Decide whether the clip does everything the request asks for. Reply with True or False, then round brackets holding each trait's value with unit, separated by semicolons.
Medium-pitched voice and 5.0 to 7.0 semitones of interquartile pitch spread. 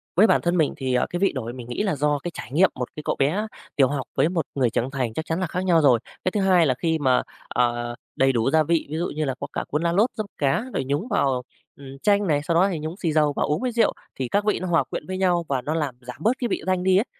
True (155 Hz; 5.5 semitones)